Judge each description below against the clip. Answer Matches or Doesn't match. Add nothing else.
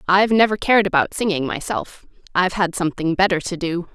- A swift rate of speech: Doesn't match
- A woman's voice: Matches